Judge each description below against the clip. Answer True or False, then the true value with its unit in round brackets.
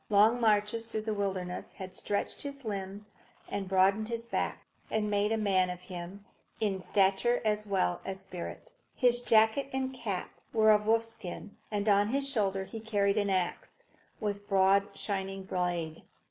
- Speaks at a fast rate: False (165 wpm)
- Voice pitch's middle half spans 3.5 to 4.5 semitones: False (2.4 semitones)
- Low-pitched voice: False (205 Hz)